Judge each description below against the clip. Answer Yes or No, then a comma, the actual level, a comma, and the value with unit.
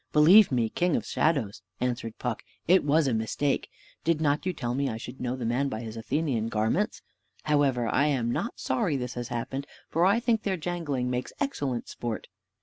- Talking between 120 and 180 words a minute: No, average, 195 wpm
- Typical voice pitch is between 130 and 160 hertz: Yes, low, 135 Hz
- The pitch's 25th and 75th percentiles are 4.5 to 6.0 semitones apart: Yes, average, 5.0 semitones